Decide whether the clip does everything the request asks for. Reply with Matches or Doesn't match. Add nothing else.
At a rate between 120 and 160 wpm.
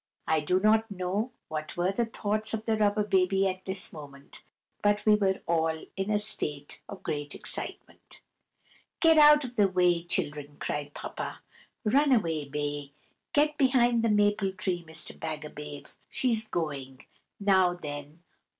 Matches